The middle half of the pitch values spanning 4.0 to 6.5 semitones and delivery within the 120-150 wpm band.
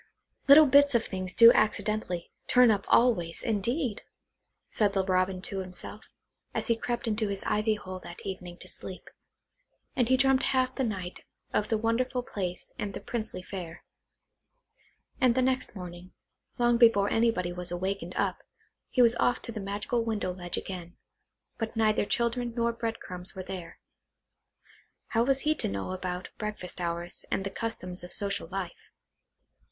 No: average, 4.3 semitones; average, 165 wpm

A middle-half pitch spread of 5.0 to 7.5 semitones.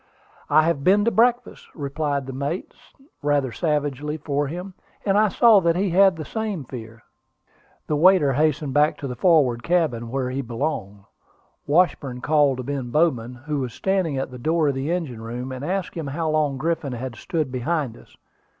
No: average, 4.4 semitones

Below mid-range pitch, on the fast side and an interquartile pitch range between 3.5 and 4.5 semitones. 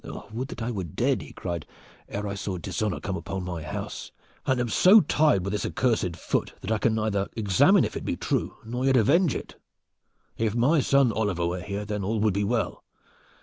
Yes: low, 105 Hz; fast, 210 wpm; average, 4.1 semitones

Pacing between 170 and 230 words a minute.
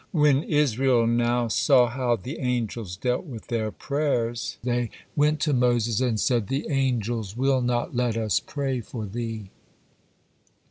No: average, 145 wpm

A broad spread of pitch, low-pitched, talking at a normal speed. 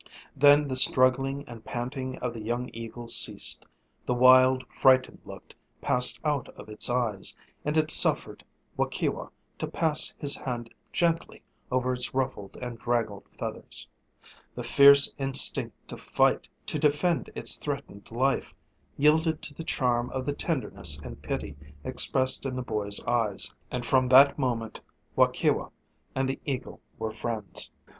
No: average, 2.8 semitones; low, 130 Hz; average, 145 wpm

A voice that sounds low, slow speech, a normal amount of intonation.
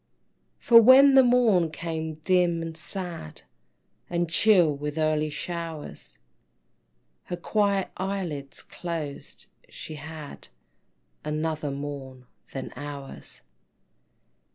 No: medium, 160 Hz; slow, 95 wpm; average, 3.7 semitones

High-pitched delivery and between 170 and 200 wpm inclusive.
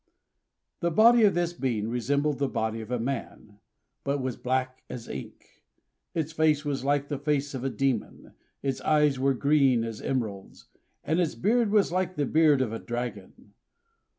No: medium, 140 Hz; average, 175 wpm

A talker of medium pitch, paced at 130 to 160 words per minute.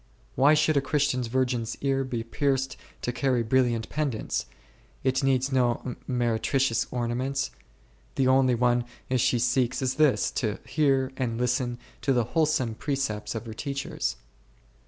No: low, 130 Hz; average, 145 wpm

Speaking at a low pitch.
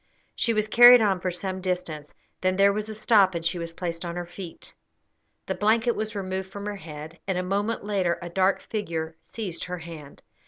No: medium, 185 Hz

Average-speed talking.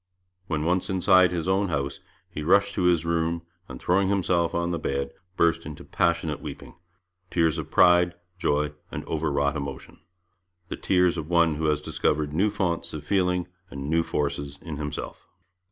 Yes: average, 170 wpm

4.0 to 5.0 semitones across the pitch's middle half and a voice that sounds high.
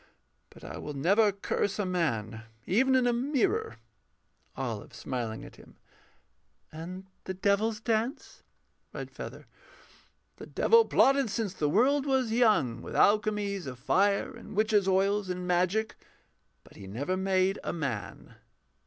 Yes: average, 4.3 semitones; high, 200 Hz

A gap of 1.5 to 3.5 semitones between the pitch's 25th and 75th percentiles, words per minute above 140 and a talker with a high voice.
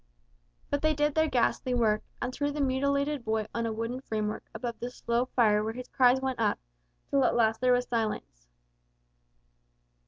Yes: average, 3.1 semitones; average, 180 wpm; high, 245 Hz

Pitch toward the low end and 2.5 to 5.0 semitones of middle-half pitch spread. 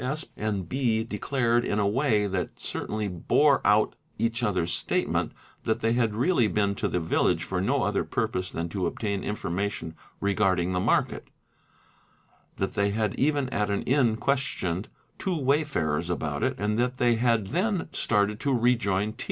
Yes: low, 110 Hz; average, 4.2 semitones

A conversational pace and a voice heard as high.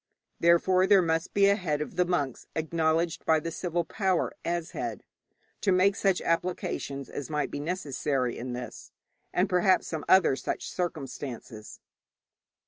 No: average, 150 wpm; medium, 165 Hz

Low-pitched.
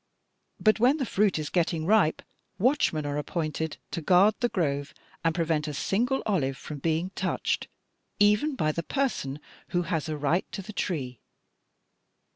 No: medium, 170 Hz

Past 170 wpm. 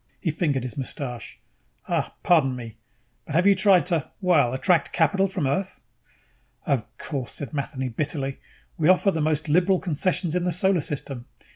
No: average, 165 wpm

